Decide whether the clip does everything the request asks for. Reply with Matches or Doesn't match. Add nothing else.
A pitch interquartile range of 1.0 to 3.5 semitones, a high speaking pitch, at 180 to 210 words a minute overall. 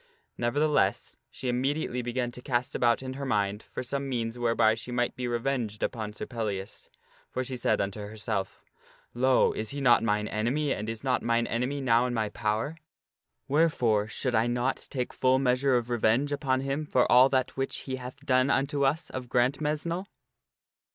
Doesn't match